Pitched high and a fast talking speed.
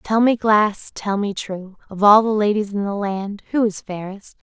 Yes: high, 205 Hz; fast, 215 wpm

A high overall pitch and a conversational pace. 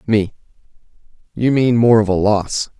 No: low, 110 Hz; average, 150 wpm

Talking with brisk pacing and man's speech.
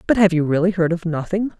No: fast, 265 wpm; female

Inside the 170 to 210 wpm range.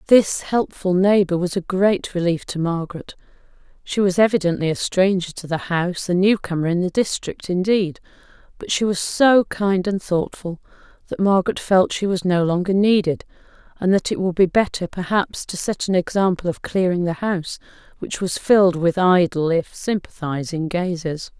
Yes: average, 175 wpm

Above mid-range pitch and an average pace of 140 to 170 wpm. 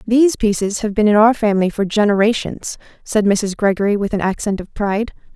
No: high, 210 Hz; average, 190 wpm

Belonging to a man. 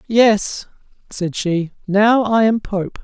Yes: male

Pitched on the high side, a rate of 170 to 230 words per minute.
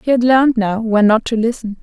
No: high, 230 Hz; fast, 265 wpm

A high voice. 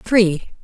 Yes: high, 200 Hz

